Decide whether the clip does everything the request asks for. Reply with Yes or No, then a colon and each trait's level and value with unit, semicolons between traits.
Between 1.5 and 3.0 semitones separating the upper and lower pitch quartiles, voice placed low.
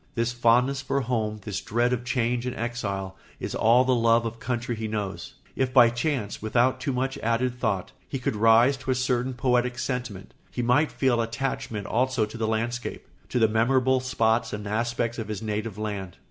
Yes: narrow, 2.4 semitones; low, 120 Hz